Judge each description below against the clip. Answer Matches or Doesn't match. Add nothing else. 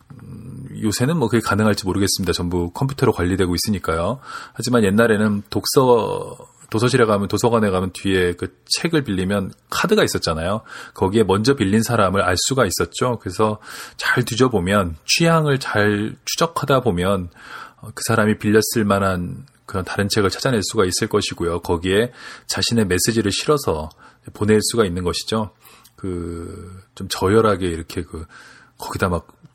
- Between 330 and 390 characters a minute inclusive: Matches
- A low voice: Matches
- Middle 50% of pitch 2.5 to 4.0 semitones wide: Matches